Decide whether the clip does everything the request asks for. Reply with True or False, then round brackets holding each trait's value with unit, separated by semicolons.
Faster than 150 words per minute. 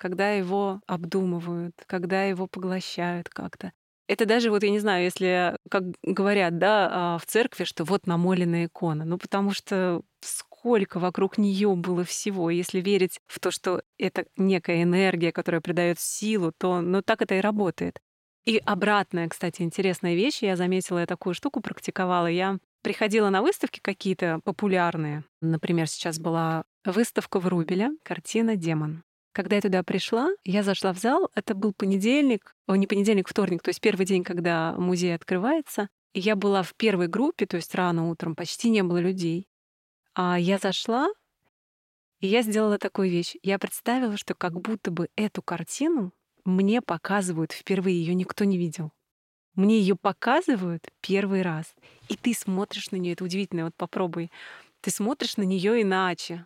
True (160 wpm)